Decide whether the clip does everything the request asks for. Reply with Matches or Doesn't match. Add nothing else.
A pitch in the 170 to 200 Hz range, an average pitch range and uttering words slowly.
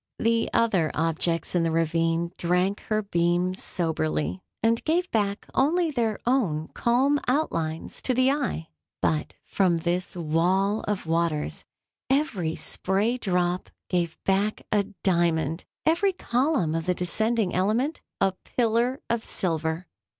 Doesn't match